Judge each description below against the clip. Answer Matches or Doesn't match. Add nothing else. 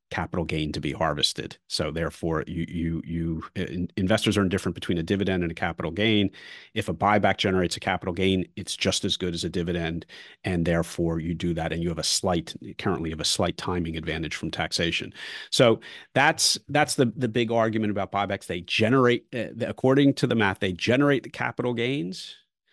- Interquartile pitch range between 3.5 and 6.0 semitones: Matches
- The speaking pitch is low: Matches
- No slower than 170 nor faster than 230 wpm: Matches